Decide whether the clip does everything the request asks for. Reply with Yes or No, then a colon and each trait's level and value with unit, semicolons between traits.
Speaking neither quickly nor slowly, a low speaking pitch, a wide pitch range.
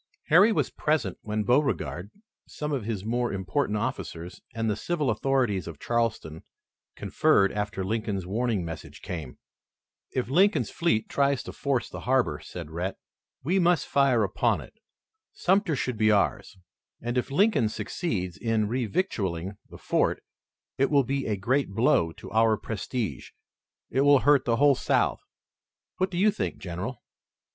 Yes: average, 150 wpm; low, 115 Hz; wide, 5.9 semitones